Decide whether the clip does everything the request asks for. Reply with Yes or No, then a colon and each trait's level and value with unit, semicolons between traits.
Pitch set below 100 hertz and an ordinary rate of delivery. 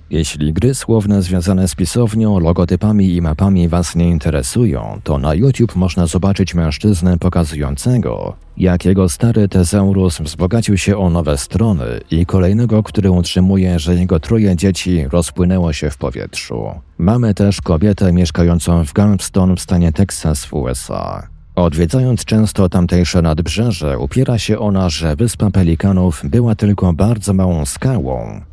Yes: very low, 90 Hz; average, 140 wpm